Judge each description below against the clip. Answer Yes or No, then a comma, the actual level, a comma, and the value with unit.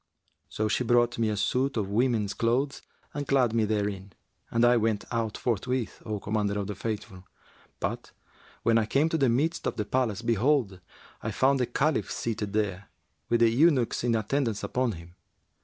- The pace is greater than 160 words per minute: Yes, average, 180 wpm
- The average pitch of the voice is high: No, low, 115 Hz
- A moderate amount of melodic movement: Yes, average, 3.3 semitones